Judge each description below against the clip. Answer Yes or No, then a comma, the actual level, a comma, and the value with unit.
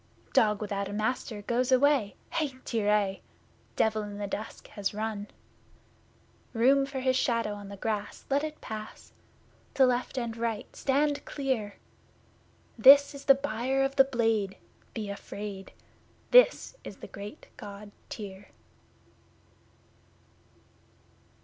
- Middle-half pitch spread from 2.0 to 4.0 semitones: No, average, 4.5 semitones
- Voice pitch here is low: No, high, 225 Hz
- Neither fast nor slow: No, slow, 130 wpm